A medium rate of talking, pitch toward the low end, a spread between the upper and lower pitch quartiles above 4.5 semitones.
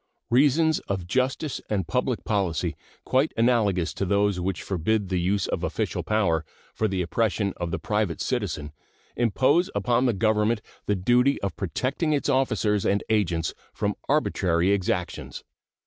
Yes: average, 145 wpm; low, 105 Hz; average, 5.1 semitones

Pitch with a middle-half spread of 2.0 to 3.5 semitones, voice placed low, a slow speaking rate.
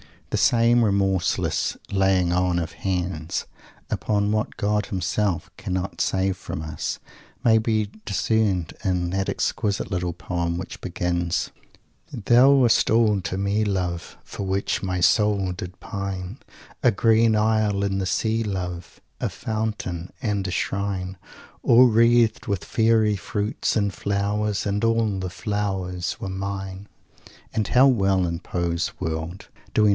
Yes: average, 2.9 semitones; low, 100 Hz; slow, 125 wpm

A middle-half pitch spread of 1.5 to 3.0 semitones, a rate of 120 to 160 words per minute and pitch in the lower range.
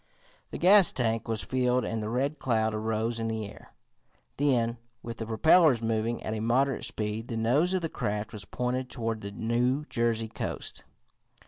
No: narrow, 2.4 semitones; average, 175 wpm; low, 115 Hz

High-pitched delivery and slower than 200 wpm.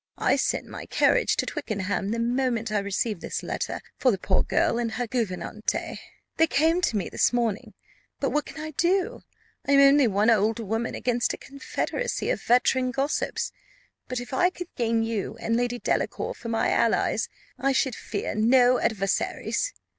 Yes: high, 240 Hz; average, 175 wpm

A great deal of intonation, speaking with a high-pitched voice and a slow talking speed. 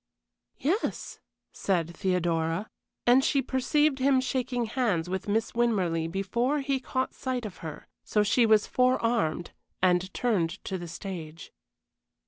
Yes: wide, 6.4 semitones; high, 215 Hz; slow, 130 wpm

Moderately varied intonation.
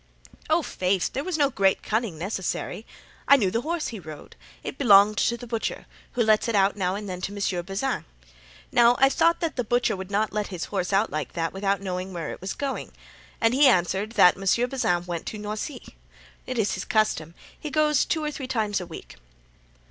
Yes: average, 4.7 semitones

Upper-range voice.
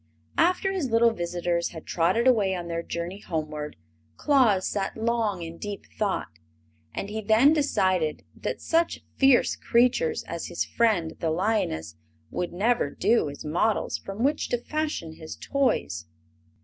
Yes: high, 205 Hz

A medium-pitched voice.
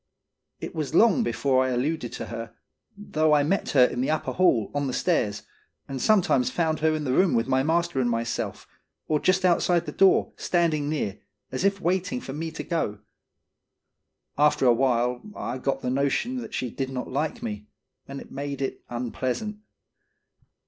Yes: medium, 145 Hz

